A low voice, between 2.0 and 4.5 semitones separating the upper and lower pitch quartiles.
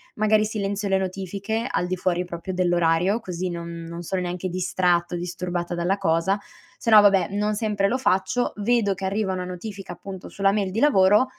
No: high, 190 Hz; narrow, 2.5 semitones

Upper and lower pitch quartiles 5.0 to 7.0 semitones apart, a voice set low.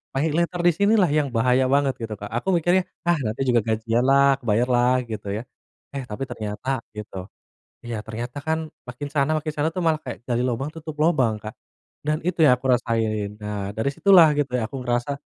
Yes: wide, 5.4 semitones; low, 130 Hz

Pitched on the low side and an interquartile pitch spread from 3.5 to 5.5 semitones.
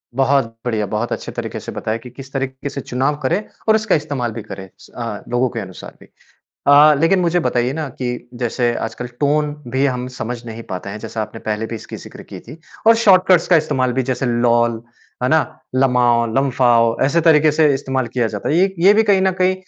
Yes: low, 130 Hz; average, 4.4 semitones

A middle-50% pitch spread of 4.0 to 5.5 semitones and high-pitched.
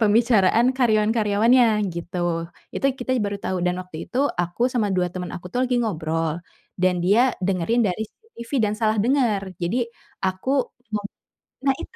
Yes: average, 4.7 semitones; high, 205 Hz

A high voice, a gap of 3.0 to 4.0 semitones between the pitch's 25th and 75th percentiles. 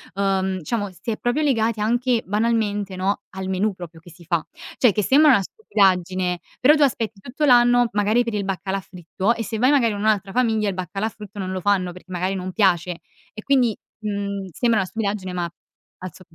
Yes: high, 205 Hz; average, 3.7 semitones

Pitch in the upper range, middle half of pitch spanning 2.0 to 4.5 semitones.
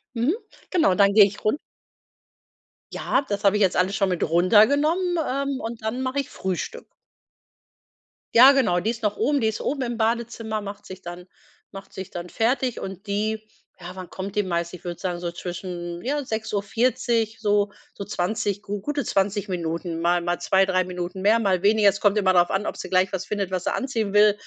Yes: high, 205 Hz; average, 3.6 semitones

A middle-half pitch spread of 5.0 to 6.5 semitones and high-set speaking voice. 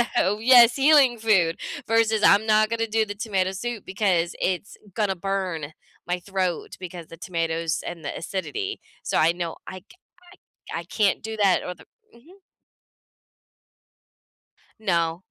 No: average, 4.3 semitones; high, 195 Hz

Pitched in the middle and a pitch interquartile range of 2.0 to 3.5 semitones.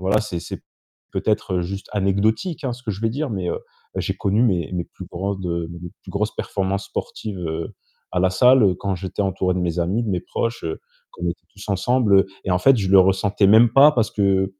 No: low, 100 Hz; average, 3.0 semitones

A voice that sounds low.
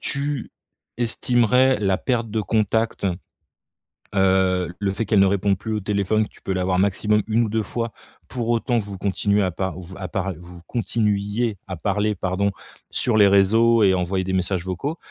Yes: low, 100 Hz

